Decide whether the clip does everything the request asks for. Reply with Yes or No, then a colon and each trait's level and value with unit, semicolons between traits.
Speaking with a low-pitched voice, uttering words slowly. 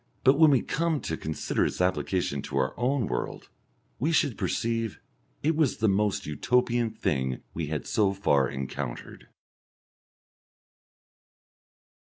Yes: low, 105 Hz; slow, 130 wpm